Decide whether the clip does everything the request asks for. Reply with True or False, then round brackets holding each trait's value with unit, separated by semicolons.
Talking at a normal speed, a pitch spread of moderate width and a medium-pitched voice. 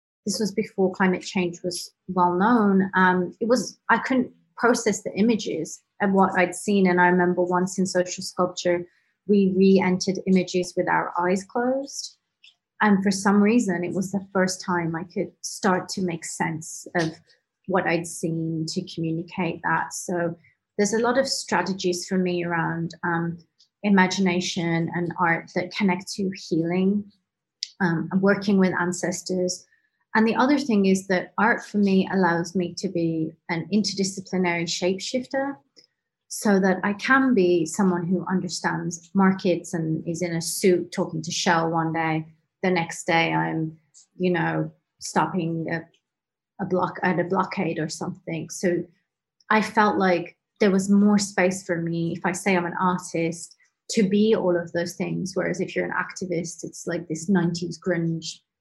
False (165 wpm; 2.2 semitones; 180 Hz)